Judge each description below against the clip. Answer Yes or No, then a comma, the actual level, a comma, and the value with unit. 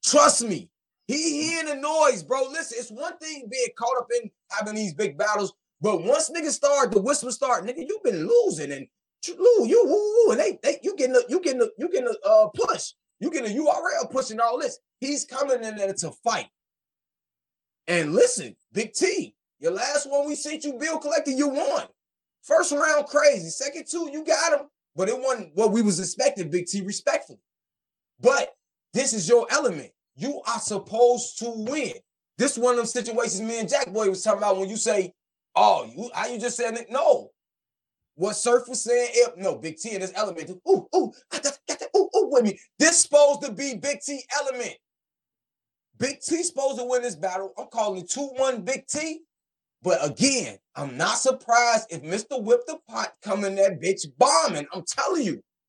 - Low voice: No, very high, 260 Hz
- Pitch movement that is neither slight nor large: No, wide, 5.7 semitones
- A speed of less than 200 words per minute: No, fast, 205 wpm